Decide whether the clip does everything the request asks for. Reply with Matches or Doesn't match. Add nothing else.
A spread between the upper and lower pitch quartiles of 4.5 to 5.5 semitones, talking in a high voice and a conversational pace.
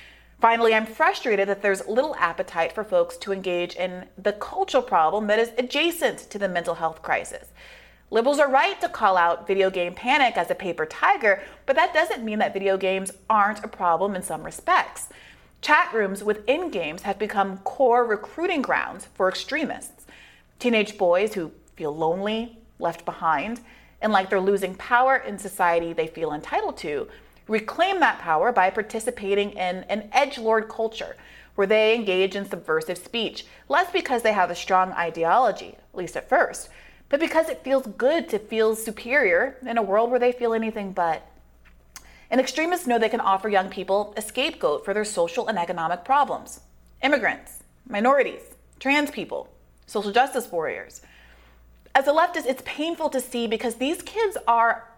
Matches